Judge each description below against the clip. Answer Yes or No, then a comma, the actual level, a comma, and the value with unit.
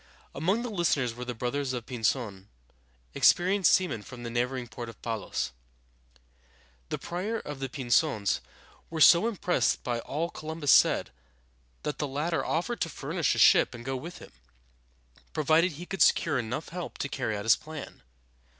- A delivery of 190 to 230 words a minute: No, average, 170 wpm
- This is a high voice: No, medium, 140 Hz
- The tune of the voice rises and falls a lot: Yes, wide, 5.9 semitones